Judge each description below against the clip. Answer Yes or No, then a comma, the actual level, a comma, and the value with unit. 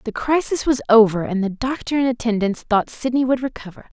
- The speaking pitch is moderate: No, high, 235 Hz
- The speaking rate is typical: Yes, average, 195 wpm